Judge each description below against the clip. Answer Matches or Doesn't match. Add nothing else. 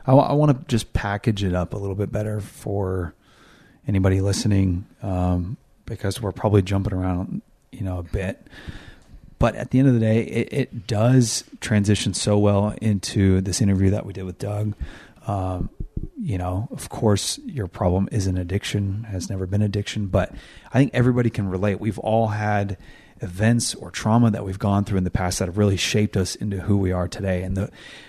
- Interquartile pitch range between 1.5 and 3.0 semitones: Matches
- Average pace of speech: Matches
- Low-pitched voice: Matches